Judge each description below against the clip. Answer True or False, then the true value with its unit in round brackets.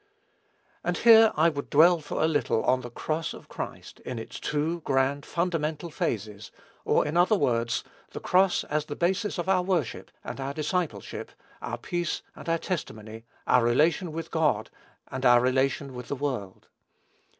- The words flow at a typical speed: True (170 wpm)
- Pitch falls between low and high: True (150 Hz)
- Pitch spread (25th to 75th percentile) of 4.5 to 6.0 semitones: True (5.1 semitones)